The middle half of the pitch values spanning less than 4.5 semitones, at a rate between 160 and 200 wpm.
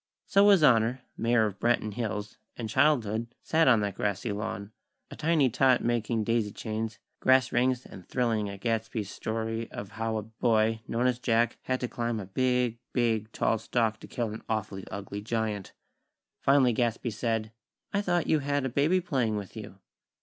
Yes: average, 2.7 semitones; average, 180 wpm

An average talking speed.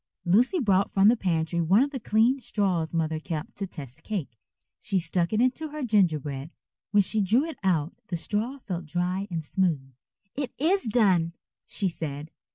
Yes: average, 175 wpm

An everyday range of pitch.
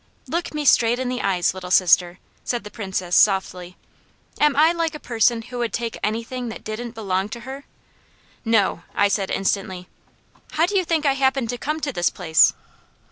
No: wide, 6.0 semitones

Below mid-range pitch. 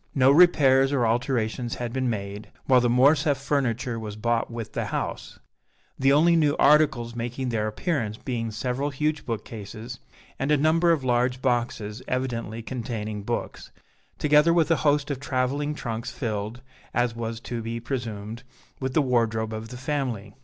Yes: low, 125 Hz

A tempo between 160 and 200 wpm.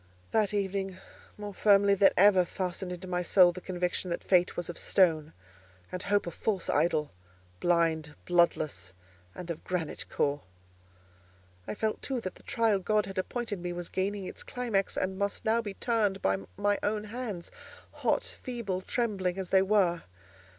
Yes: average, 165 wpm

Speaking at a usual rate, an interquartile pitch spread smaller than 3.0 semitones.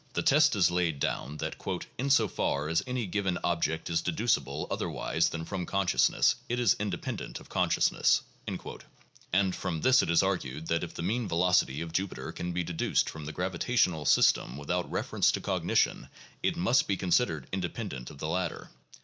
No: average, 190 wpm; average, 3.5 semitones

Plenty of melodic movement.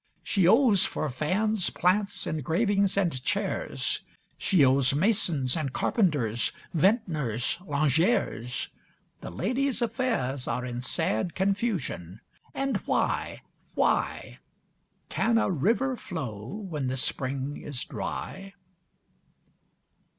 Yes: wide, 8.0 semitones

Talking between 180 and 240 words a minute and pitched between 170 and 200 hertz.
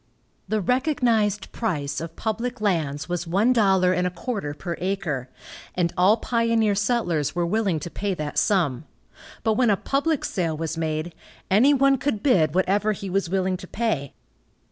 No: average, 165 wpm; high, 190 Hz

